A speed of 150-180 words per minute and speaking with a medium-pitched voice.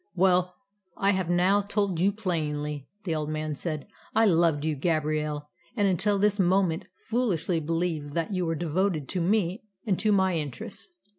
Yes: average, 165 wpm; medium, 175 Hz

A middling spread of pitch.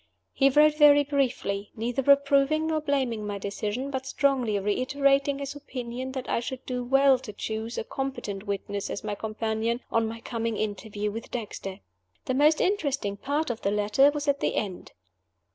Yes: average, 4.5 semitones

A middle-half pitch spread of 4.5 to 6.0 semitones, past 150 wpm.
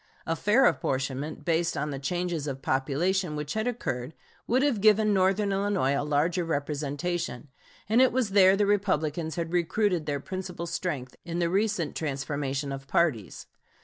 Yes: wide, 5.4 semitones; average, 160 wpm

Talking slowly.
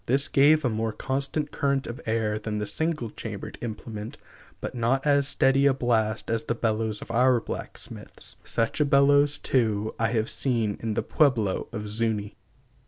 No: average, 170 wpm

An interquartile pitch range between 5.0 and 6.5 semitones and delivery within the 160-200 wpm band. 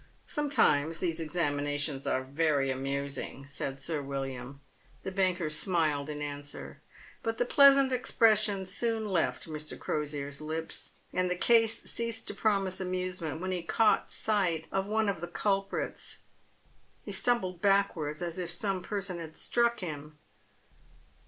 No: wide, 5.4 semitones; average, 145 wpm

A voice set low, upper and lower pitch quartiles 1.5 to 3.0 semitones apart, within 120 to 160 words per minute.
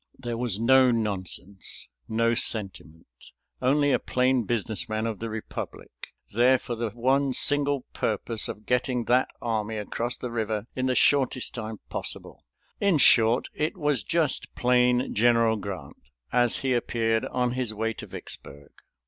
Yes: low, 120 Hz; narrow, 2.6 semitones; average, 150 wpm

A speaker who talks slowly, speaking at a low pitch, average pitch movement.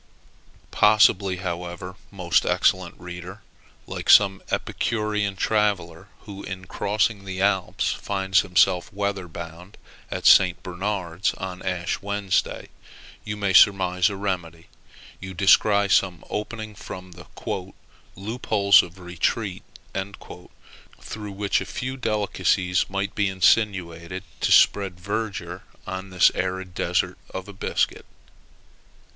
No: slow, 110 wpm; very low, 95 Hz; narrow, 2.1 semitones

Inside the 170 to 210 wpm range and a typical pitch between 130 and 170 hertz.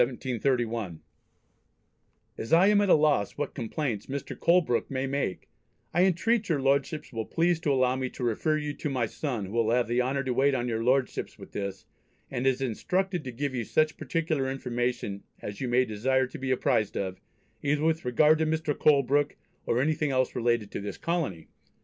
Yes: average, 190 wpm; low, 135 Hz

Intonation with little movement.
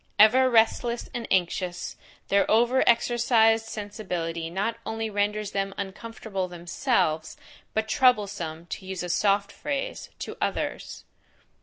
No: average, 3.6 semitones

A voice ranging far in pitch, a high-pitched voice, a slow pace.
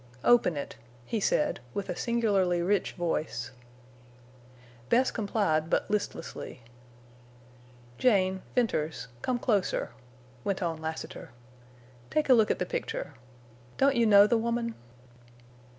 Yes: wide, 6.0 semitones; high, 200 Hz; slow, 110 wpm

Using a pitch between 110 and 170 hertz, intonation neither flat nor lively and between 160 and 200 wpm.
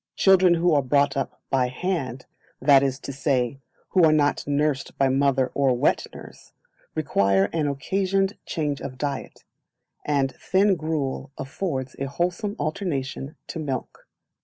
No: medium, 140 Hz; average, 3.8 semitones; average, 145 wpm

